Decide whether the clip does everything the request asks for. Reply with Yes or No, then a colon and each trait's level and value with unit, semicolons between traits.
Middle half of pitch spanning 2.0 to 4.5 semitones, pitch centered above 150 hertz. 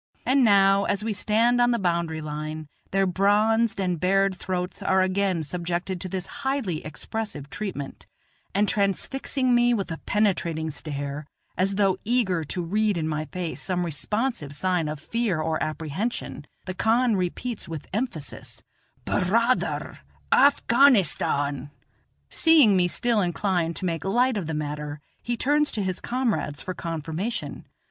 No: wide, 5.5 semitones; high, 190 Hz